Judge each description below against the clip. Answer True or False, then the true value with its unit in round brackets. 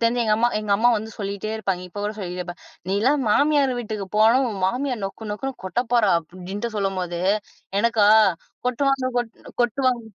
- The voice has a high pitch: True (215 Hz)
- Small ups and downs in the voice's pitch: False (3.7 semitones)